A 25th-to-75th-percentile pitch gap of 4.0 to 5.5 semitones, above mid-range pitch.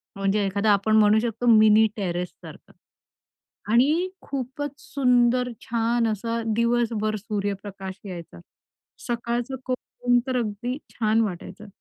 No: average, 3.0 semitones; high, 225 Hz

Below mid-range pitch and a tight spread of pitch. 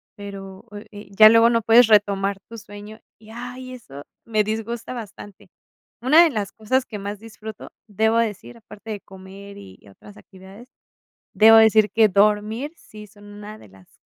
No: high, 215 Hz; narrow, 2.1 semitones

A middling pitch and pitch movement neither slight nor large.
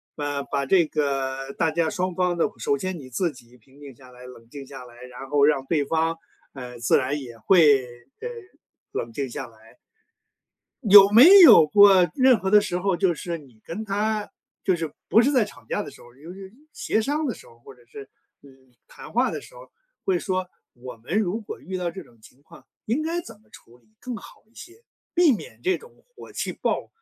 No: medium, 165 Hz; wide, 7.7 semitones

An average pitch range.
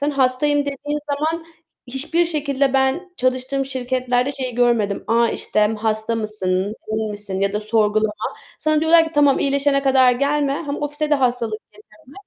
Yes: average, 4.7 semitones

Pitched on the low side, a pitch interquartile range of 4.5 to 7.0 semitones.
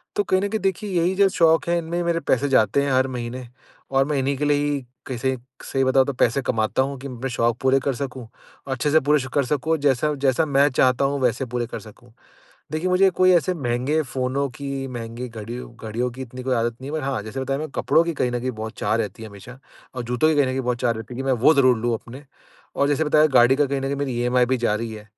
No: low, 130 Hz; average, 3.1 semitones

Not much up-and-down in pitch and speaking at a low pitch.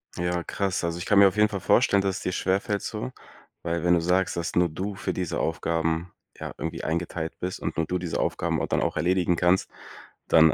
Yes: narrow, 2.1 semitones; very low, 90 Hz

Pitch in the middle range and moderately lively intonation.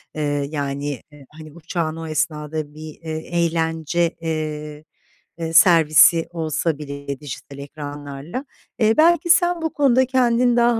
Yes: medium, 160 Hz; average, 3.0 semitones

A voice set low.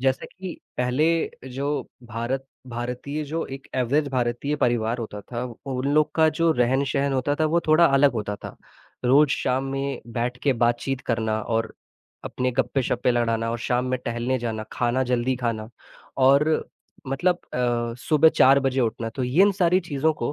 Yes: low, 130 Hz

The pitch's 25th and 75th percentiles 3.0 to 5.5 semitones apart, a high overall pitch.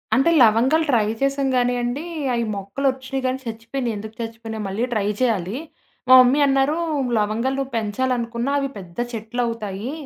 Yes: average, 3.3 semitones; high, 240 Hz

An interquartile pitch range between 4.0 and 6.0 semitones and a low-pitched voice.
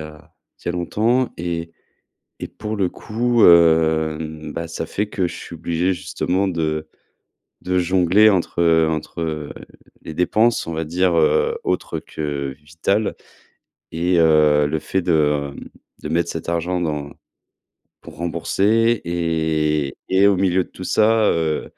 No: average, 3.1 semitones; very low, 85 Hz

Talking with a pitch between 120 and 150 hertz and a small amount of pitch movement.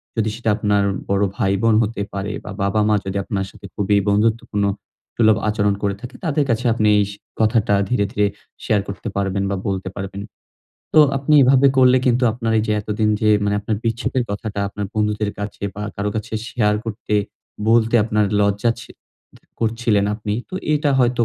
No: low, 105 Hz; narrow, 2.2 semitones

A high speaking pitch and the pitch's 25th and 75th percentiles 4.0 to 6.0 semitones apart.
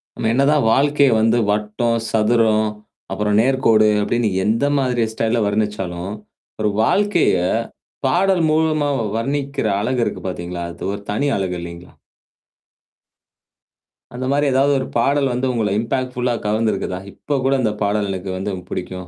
No: low, 115 Hz; average, 4.6 semitones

